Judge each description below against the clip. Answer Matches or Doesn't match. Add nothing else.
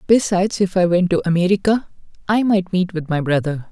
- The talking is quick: Doesn't match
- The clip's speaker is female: Doesn't match